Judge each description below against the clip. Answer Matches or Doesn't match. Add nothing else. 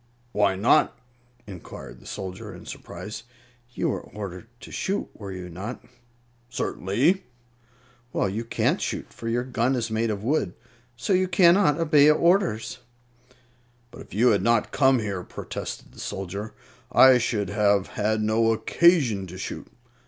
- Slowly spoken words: Doesn't match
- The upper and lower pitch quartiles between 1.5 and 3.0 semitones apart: Doesn't match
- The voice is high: Doesn't match